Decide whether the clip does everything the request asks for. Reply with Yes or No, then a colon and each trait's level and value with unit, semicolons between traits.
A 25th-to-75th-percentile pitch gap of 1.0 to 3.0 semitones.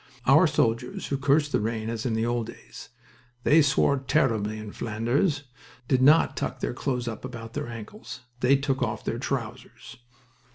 No: average, 3.5 semitones